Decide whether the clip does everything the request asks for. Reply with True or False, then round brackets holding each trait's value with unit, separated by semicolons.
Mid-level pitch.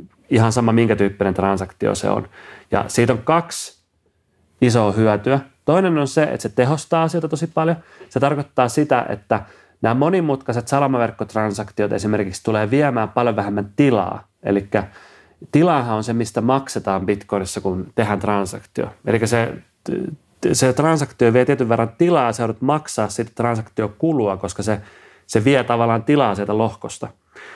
False (115 Hz)